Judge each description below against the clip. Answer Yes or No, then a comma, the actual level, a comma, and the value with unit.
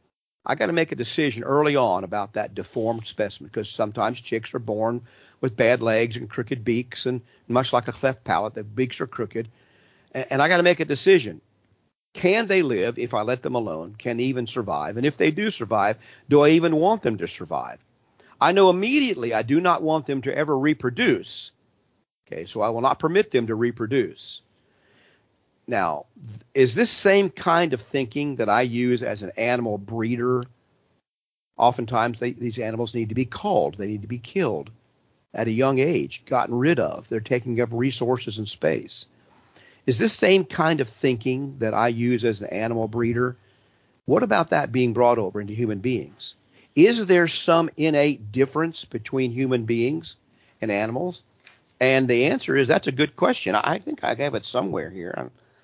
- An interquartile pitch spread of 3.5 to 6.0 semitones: Yes, average, 3.9 semitones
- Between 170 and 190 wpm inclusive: Yes, average, 185 wpm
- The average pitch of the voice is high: No, low, 125 Hz